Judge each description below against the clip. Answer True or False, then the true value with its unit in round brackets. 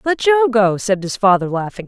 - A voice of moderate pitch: False (220 Hz)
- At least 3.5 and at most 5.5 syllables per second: True (5.0 syllables/s)